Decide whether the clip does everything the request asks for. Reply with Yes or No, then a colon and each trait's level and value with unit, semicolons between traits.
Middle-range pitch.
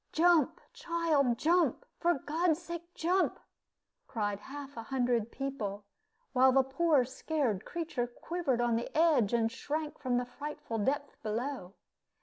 No: very high, 270 Hz